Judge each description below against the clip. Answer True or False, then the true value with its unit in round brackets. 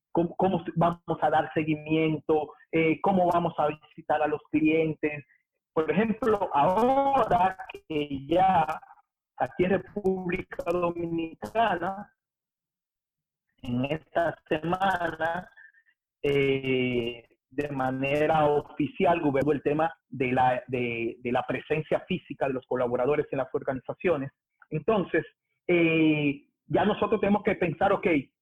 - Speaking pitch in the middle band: True (160 Hz)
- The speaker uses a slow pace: True (115 wpm)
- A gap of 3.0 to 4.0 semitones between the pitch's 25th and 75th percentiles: True (3.7 semitones)